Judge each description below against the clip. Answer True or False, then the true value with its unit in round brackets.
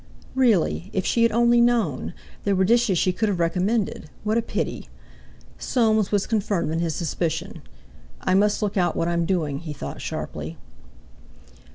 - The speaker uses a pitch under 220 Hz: True (190 Hz)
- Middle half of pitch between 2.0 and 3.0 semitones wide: False (4.7 semitones)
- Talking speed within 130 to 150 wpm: False (165 wpm)